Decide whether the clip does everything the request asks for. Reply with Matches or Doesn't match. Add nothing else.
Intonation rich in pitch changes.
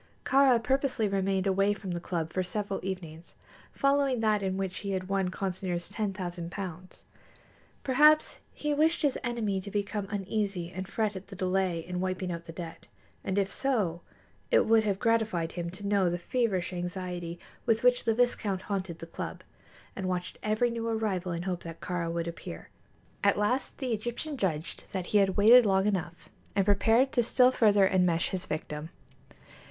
Doesn't match